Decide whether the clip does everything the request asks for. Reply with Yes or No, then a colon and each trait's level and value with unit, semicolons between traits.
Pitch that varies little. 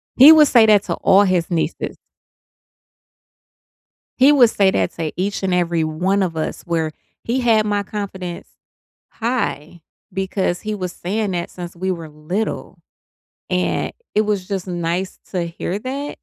No: average, 3.6 semitones